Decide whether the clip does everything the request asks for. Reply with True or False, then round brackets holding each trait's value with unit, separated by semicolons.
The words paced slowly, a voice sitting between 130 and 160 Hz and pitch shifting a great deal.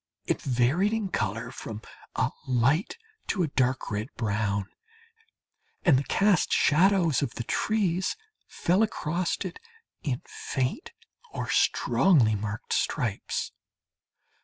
True (115 wpm; 140 Hz; 8.0 semitones)